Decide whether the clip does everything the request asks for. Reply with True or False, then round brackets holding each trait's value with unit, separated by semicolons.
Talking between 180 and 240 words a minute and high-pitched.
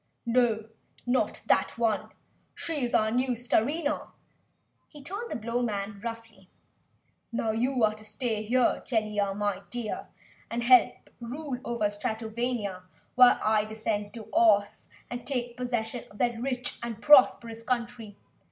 False (145 wpm; 235 Hz)